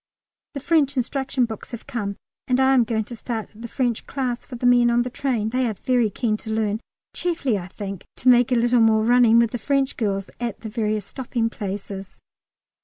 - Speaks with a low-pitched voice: No, high, 235 Hz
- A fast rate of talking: Yes, fast, 210 wpm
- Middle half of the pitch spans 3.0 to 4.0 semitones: No, narrow, 2.6 semitones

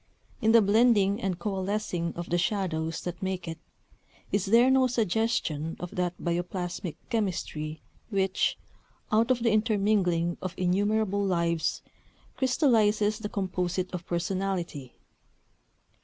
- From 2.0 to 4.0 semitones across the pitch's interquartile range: Yes, average, 3.7 semitones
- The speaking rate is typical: No, slow, 120 wpm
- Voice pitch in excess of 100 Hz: Yes, high, 190 Hz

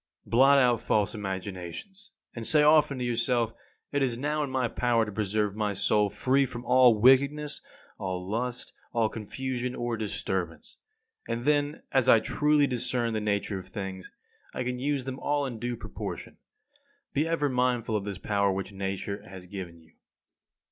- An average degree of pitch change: Yes, average, 4.5 semitones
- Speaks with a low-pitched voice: Yes, low, 120 Hz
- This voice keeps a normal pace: Yes, average, 170 wpm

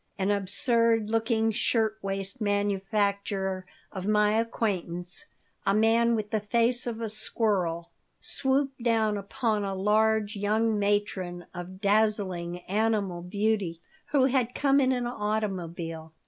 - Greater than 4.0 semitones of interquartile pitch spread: No, average, 2.7 semitones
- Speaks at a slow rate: Yes, slow, 125 wpm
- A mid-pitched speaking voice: No, high, 210 Hz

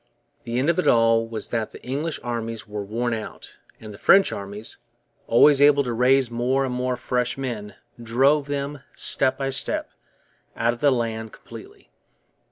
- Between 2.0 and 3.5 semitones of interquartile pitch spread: Yes, average, 3.0 semitones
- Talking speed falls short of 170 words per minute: No, average, 175 wpm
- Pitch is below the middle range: Yes, low, 120 Hz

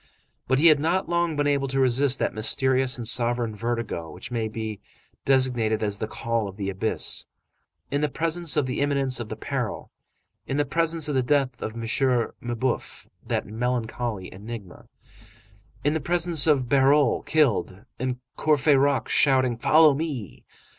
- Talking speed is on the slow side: No, average, 160 wpm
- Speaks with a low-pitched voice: Yes, low, 130 Hz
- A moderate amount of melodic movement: Yes, average, 4.0 semitones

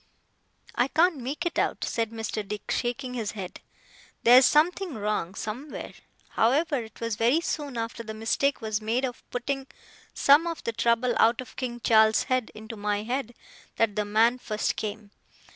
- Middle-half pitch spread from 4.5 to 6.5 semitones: No, average, 3.5 semitones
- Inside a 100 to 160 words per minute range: No, average, 170 wpm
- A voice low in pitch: No, high, 235 Hz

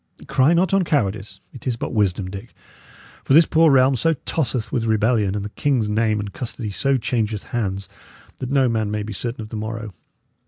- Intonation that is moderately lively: Yes, average, 4.0 semitones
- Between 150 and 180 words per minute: No, average, 200 wpm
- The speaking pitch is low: Yes, low, 115 Hz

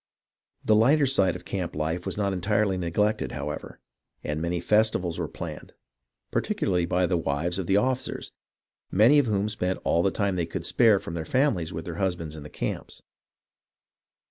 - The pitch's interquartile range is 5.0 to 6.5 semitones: No, average, 3.9 semitones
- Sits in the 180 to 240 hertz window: No, very low, 90 Hz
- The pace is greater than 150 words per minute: Yes, average, 175 wpm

